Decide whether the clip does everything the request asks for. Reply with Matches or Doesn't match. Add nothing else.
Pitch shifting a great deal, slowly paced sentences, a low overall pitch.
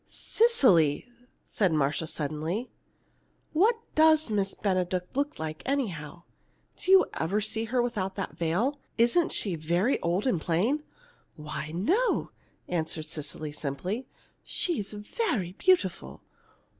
Doesn't match